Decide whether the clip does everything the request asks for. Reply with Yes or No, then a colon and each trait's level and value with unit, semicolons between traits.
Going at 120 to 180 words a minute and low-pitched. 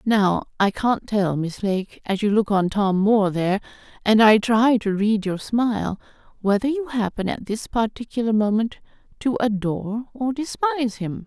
No: average, 170 wpm; high, 215 Hz